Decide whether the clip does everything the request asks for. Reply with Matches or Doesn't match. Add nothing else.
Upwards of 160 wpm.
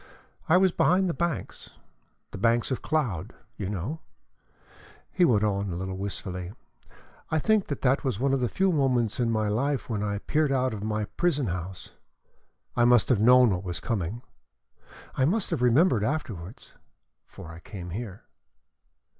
Matches